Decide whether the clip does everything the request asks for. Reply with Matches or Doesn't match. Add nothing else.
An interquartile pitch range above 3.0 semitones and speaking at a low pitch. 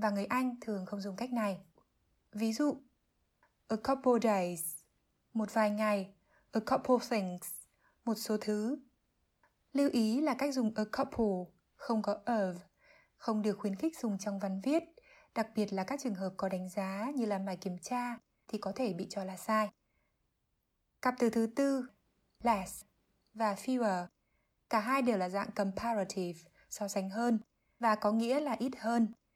Doesn't match